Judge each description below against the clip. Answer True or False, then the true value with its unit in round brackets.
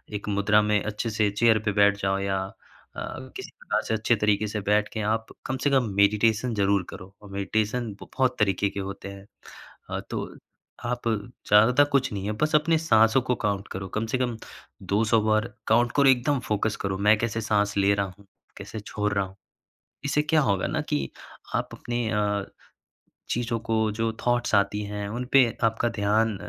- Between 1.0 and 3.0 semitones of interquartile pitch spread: True (2.7 semitones)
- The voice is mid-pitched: False (105 Hz)